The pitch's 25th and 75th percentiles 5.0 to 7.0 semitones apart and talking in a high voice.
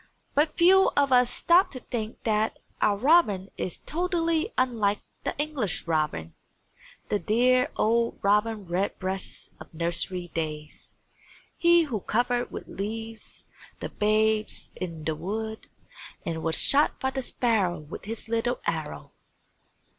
Yes: wide, 5.6 semitones; high, 220 Hz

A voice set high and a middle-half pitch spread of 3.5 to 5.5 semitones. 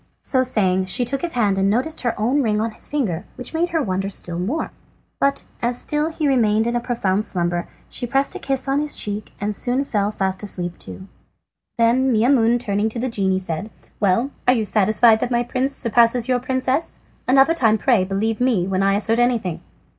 Yes: high, 230 Hz; average, 4.4 semitones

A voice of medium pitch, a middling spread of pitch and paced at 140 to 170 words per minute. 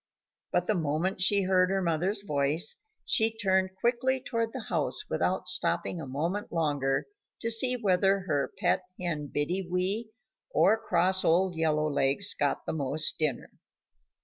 Yes: medium, 180 Hz; average, 4.6 semitones; average, 150 wpm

